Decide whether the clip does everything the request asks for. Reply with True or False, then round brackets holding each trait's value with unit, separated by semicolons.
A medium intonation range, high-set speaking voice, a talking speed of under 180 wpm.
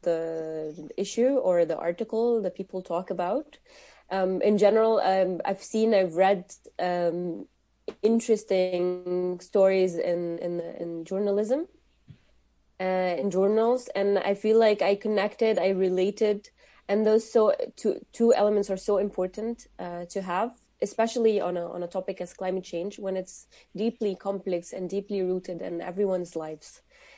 True (3.2 semitones; 195 Hz; 145 wpm)